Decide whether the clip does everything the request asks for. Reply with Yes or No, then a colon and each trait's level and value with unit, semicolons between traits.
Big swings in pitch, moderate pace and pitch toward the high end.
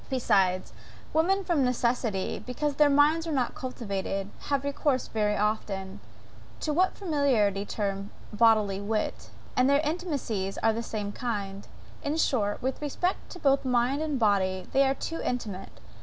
Yes: wide, 6.0 semitones; average, 155 wpm; high, 245 Hz